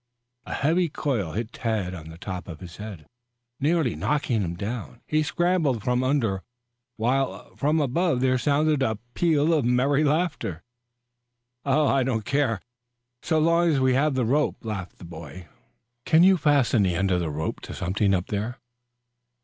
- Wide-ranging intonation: Yes, wide, 7.0 semitones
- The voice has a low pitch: Yes, low, 125 Hz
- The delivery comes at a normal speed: Yes, average, 165 wpm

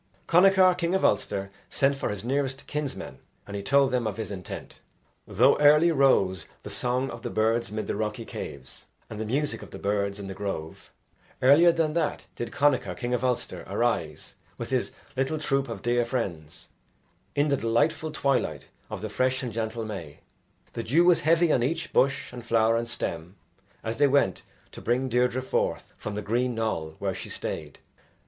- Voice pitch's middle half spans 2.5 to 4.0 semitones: No, average, 4.8 semitones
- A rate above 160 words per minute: Yes, average, 185 wpm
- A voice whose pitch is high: No, low, 125 Hz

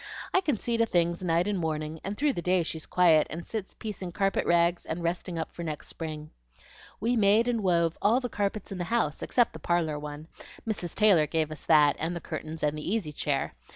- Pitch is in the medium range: Yes, medium, 175 Hz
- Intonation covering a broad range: No, average, 4.5 semitones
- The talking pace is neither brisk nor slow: No, fast, 220 wpm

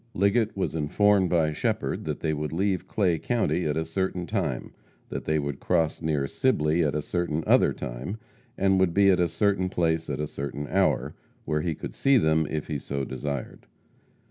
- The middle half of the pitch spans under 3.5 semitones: No, average, 4.0 semitones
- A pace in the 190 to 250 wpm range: Yes, average, 195 wpm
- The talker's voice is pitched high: No, very low, 80 Hz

